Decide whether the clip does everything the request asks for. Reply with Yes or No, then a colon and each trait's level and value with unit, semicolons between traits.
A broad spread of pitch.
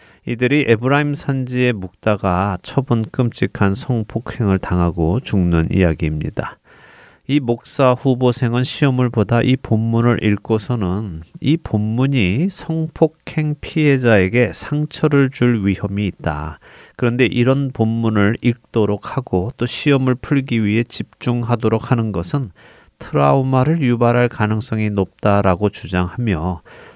No: average, 4.4 semitones